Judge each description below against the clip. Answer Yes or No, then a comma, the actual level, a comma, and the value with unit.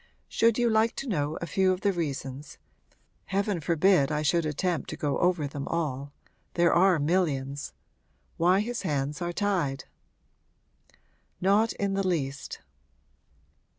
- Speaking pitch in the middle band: Yes, medium, 170 Hz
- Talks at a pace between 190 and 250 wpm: No, average, 140 wpm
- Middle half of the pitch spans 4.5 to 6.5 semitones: Yes, average, 5.0 semitones